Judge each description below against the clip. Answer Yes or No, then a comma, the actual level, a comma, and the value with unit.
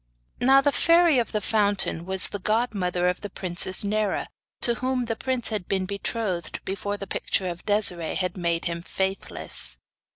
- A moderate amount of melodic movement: Yes, average, 3.9 semitones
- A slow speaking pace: No, average, 170 wpm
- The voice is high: Yes, high, 200 Hz